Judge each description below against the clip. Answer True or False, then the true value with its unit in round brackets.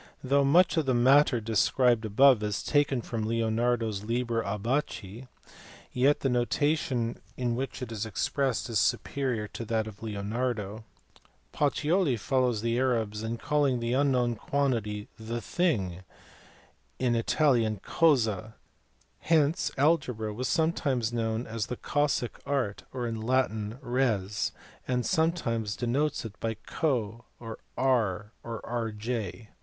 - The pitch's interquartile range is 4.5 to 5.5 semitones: False (3.4 semitones)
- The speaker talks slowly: True (130 wpm)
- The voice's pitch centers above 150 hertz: False (120 Hz)